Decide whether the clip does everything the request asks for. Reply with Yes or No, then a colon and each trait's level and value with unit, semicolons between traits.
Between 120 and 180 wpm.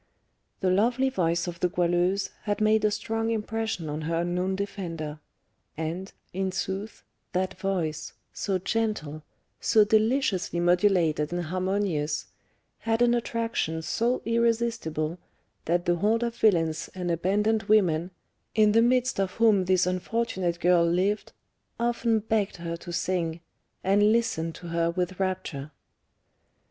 Yes: slow, 135 wpm